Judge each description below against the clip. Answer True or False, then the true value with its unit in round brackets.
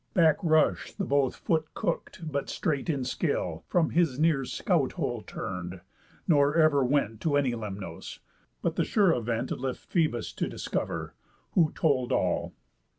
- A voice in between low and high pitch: True (145 Hz)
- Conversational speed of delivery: True (150 wpm)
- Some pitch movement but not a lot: True (4.7 semitones)